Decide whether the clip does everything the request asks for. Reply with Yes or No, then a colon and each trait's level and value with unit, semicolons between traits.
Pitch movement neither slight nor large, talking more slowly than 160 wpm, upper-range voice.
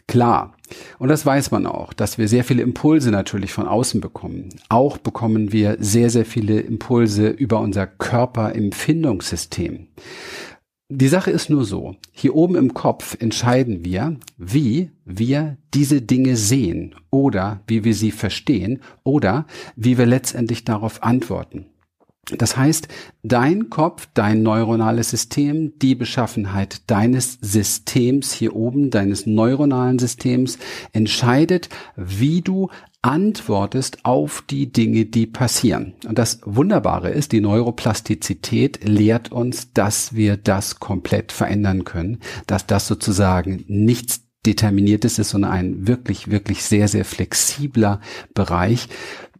No: average, 3.6 semitones; average, 130 wpm; low, 115 Hz